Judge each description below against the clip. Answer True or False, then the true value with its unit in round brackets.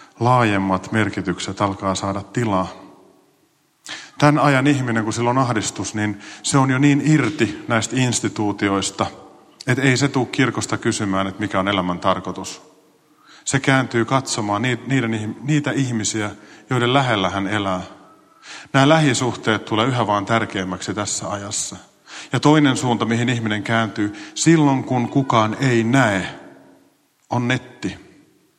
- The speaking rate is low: False (130 wpm)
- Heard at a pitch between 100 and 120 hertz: True (115 Hz)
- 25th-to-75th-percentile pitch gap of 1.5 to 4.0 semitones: False (4.4 semitones)